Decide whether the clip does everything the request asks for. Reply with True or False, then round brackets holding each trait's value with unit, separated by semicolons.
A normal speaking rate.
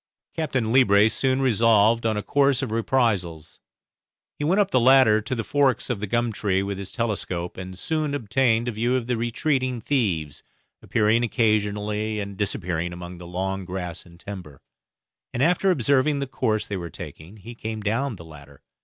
True (180 wpm)